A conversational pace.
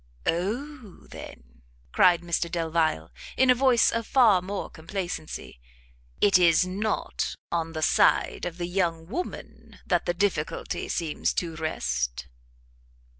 No: slow, 125 wpm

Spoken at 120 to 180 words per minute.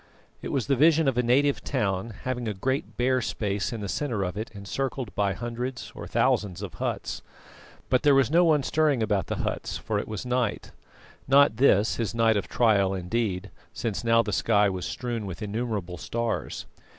No: average, 190 wpm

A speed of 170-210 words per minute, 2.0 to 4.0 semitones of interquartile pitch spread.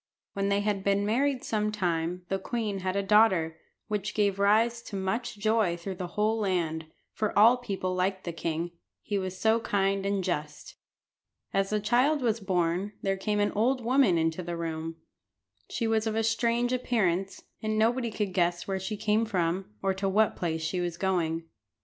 Yes: average, 185 wpm; average, 3.4 semitones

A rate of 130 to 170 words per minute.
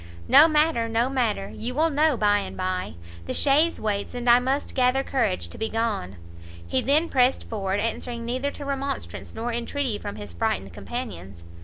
No: average, 180 wpm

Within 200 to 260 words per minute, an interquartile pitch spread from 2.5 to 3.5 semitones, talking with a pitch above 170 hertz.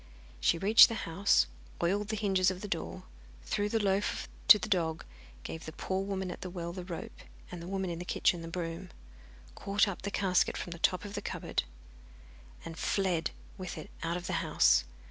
Yes: fast, 205 wpm; average, 3.0 semitones; medium, 185 Hz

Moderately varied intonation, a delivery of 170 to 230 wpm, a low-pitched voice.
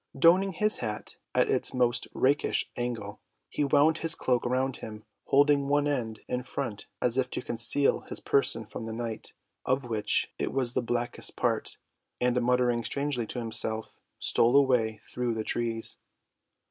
No: average, 3.3 semitones; average, 160 wpm; low, 125 Hz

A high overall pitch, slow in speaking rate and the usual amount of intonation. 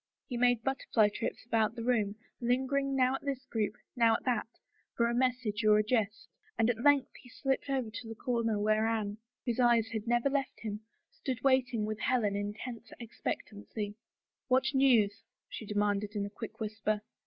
No: high, 230 Hz; average, 190 wpm; average, 3.0 semitones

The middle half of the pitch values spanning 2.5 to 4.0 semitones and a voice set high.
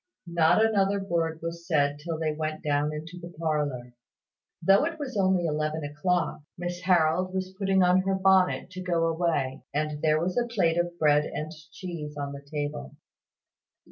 No: average, 3.3 semitones; medium, 165 Hz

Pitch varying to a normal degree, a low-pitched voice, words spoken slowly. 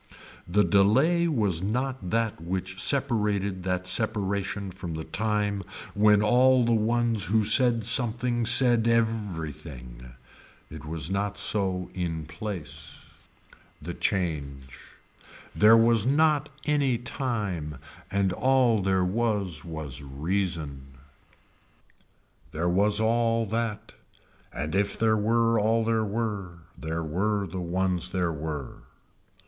Yes: average, 4.7 semitones; low, 100 Hz; slow, 120 wpm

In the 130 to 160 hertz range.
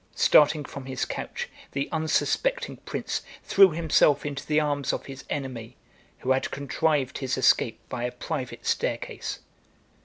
Yes: medium, 140 Hz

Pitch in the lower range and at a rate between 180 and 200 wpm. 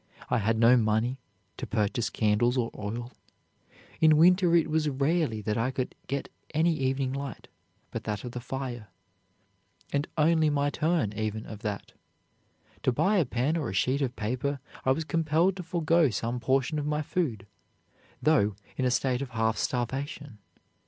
No: low, 130 Hz; average, 170 wpm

